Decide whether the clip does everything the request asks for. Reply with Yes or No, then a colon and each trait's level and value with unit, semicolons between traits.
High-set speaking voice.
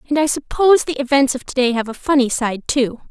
Yes: very high, 265 Hz